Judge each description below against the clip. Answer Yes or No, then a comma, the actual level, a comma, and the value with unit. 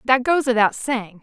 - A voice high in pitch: Yes, high, 240 Hz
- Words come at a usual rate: Yes, average, 195 wpm